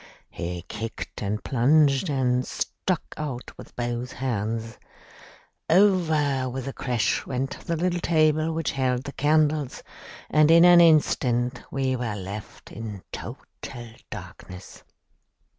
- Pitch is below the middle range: Yes, low, 130 Hz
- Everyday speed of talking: No, slow, 125 wpm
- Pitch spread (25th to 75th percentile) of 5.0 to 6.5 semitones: No, average, 4.6 semitones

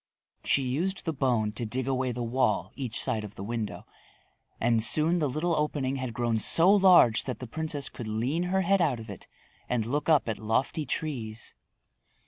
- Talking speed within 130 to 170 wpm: No, average, 190 wpm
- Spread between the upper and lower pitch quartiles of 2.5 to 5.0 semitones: No, wide, 5.4 semitones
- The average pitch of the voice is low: Yes, low, 130 Hz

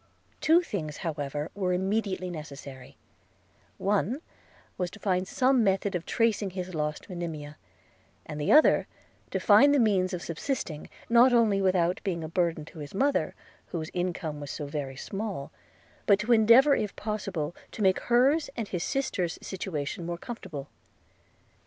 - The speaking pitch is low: No, medium, 185 Hz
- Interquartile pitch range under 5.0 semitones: No, wide, 5.4 semitones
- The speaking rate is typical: Yes, average, 150 wpm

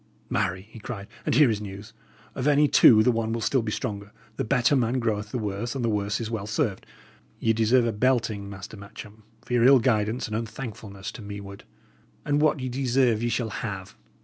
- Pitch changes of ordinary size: Yes, average, 3.3 semitones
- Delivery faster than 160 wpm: Yes, fast, 205 wpm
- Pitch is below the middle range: Yes, low, 115 Hz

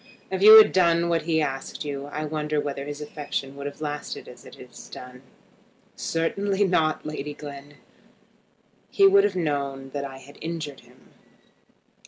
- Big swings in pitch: No, average, 3.0 semitones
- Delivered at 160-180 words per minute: Yes, average, 165 wpm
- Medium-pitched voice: Yes, medium, 150 Hz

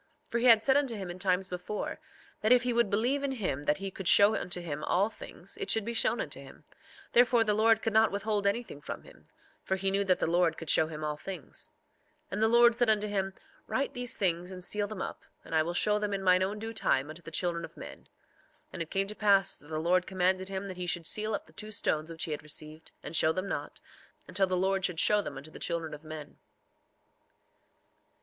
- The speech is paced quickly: Yes, fast, 250 wpm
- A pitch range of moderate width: Yes, average, 4.1 semitones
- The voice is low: No, high, 195 Hz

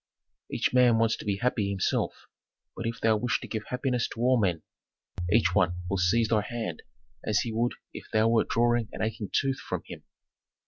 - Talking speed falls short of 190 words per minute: No, average, 195 wpm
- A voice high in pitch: No, low, 115 Hz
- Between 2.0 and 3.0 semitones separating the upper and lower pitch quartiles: Yes, narrow, 2.4 semitones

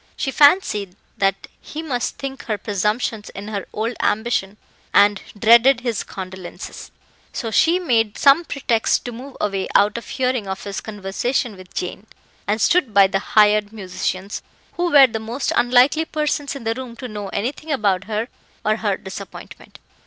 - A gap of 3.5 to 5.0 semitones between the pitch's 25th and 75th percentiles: Yes, average, 4.3 semitones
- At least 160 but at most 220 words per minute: Yes, average, 165 wpm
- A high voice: Yes, high, 220 Hz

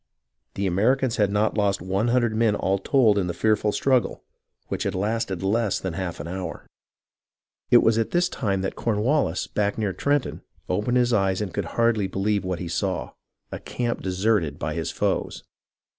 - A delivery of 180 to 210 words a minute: Yes, average, 185 wpm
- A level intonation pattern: No, average, 3.5 semitones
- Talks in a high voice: No, low, 105 Hz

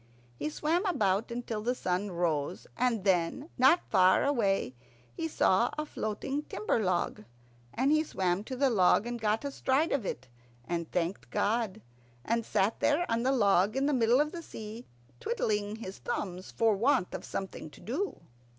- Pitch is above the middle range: Yes, high, 220 Hz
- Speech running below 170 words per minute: No, average, 175 wpm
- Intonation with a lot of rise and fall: Yes, wide, 5.8 semitones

